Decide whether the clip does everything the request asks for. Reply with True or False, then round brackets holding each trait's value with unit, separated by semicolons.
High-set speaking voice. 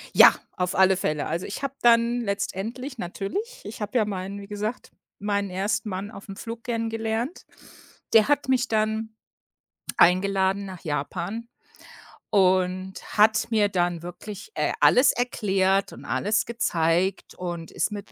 True (205 Hz)